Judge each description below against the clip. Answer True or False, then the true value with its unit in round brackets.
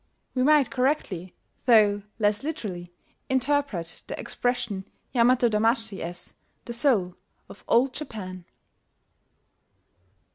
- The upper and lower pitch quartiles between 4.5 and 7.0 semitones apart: True (5.1 semitones)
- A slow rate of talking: True (100 wpm)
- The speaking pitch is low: False (230 Hz)